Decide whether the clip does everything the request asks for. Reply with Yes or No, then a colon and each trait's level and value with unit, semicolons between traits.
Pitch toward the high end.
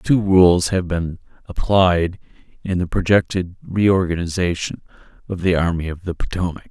No: very low, 90 Hz